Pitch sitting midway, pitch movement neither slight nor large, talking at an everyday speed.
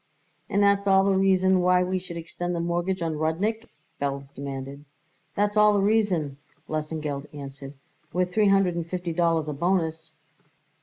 Yes: medium, 175 Hz; average, 3.8 semitones; average, 160 wpm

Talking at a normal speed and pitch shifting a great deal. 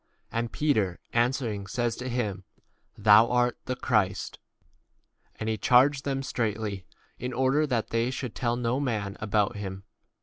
No: average, 165 wpm; average, 3.3 semitones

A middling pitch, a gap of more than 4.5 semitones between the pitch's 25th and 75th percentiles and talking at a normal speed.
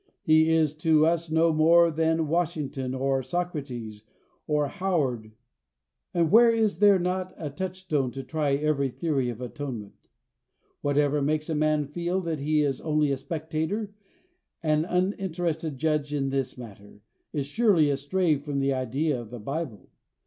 No: medium, 155 Hz; average, 3.4 semitones; average, 150 wpm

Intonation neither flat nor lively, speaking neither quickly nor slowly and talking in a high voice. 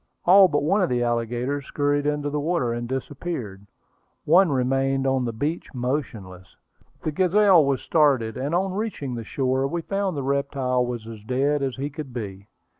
No: average, 3.7 semitones; average, 180 wpm; low, 135 Hz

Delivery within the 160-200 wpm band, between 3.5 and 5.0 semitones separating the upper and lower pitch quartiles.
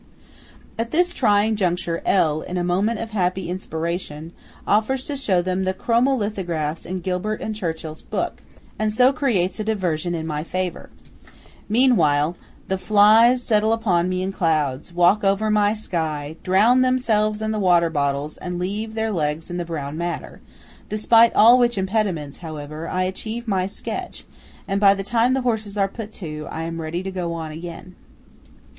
Yes: average, 170 wpm; average, 4.5 semitones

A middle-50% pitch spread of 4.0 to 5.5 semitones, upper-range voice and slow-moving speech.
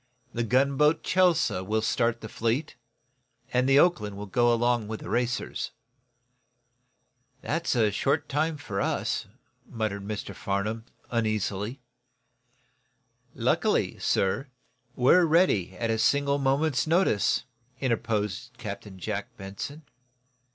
No: average, 5.0 semitones; low, 120 Hz; slow, 110 wpm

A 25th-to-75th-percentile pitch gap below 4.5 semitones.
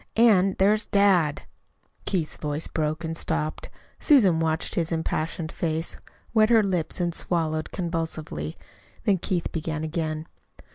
Yes: average, 3.3 semitones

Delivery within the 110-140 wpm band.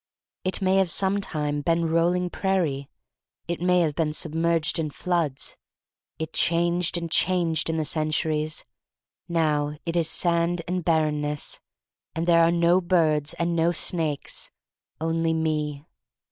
Yes: slow, 135 wpm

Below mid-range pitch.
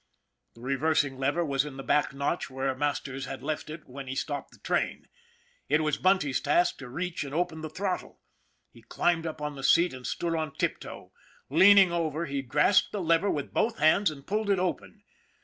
No: medium, 155 Hz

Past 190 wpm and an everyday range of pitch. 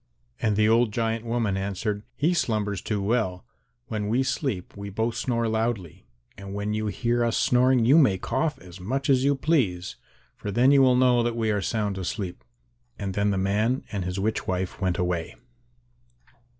No: average, 180 wpm; average, 3.7 semitones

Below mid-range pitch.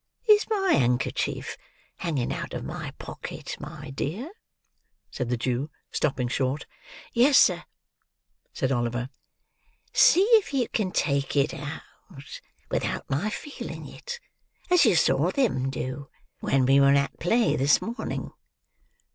No: medium, 145 Hz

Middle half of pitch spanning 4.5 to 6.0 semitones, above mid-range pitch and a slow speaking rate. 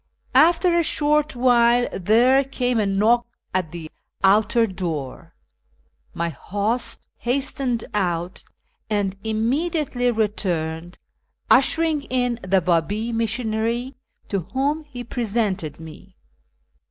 Yes: average, 4.9 semitones; high, 225 Hz; slow, 105 wpm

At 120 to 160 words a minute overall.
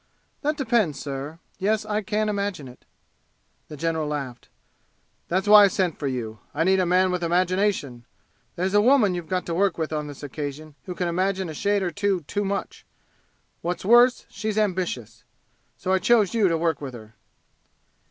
No: average, 180 wpm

